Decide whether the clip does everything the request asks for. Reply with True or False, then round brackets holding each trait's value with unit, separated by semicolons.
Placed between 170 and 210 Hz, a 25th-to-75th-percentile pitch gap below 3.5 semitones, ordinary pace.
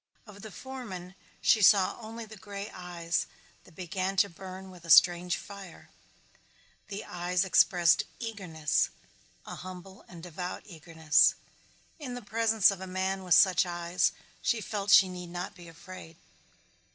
True (185 Hz; 2.5 semitones; 150 wpm)